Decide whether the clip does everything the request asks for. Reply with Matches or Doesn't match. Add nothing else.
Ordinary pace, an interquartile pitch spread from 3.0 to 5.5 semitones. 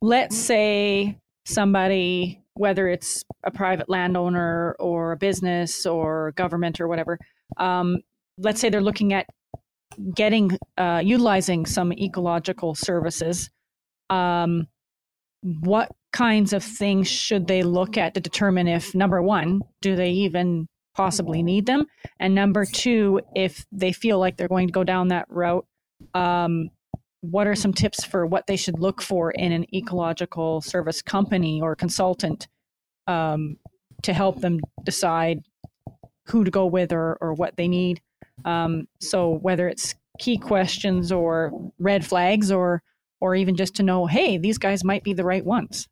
Doesn't match